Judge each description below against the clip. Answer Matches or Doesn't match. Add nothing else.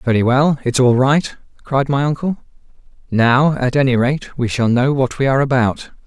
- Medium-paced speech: Matches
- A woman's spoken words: Doesn't match